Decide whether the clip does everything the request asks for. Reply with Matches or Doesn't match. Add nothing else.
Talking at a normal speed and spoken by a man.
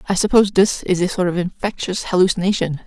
Doesn't match